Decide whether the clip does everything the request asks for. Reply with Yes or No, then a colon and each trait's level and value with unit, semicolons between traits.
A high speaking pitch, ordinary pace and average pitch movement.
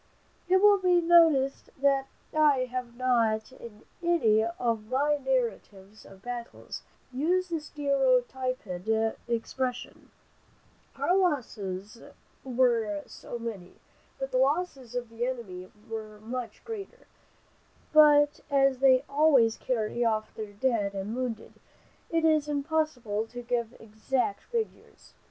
No: very high, 255 Hz; slow, 120 wpm; average, 4.5 semitones